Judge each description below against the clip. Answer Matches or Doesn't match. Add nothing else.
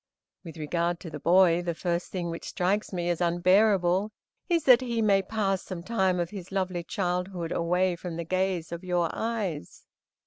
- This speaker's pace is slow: Doesn't match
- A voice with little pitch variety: Matches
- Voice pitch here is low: Doesn't match